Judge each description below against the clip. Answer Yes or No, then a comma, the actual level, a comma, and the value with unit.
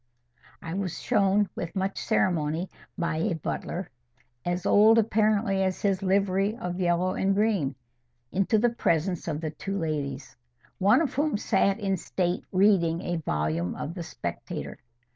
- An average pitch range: Yes, average, 3.3 semitones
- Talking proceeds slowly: No, average, 150 wpm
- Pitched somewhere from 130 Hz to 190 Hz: Yes, medium, 185 Hz